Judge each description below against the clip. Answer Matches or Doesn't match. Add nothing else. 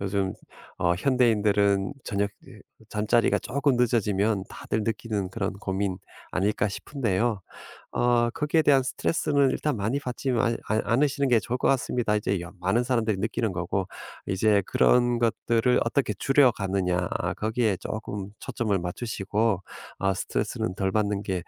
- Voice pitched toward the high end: Doesn't match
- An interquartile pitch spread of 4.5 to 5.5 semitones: Doesn't match